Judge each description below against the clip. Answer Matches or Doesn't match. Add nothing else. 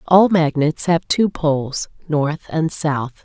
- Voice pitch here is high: Doesn't match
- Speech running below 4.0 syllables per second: Matches